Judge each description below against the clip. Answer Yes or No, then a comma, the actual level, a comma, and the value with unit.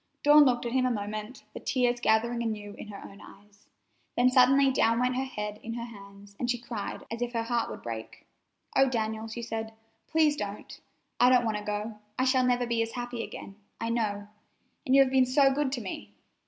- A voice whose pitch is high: Yes, high, 235 Hz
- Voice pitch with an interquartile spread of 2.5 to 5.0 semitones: Yes, average, 3.1 semitones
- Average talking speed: No, fast, 220 wpm